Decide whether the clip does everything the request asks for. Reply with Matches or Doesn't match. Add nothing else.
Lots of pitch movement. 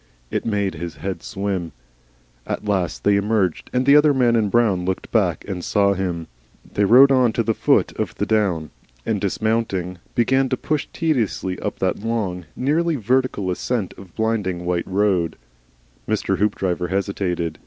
Doesn't match